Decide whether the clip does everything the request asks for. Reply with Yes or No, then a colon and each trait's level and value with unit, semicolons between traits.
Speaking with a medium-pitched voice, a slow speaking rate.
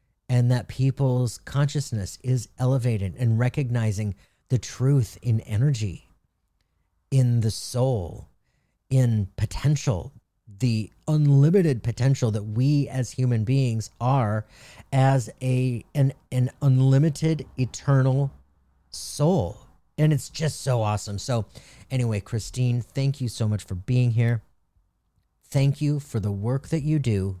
No: low, 125 Hz; slow, 125 wpm